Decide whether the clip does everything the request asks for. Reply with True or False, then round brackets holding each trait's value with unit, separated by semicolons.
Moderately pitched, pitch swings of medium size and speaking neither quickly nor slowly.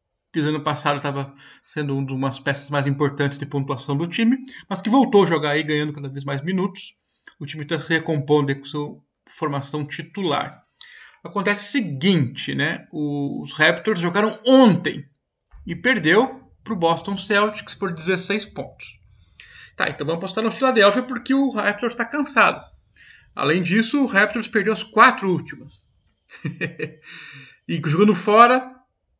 False (170 Hz; 6.8 semitones; 150 wpm)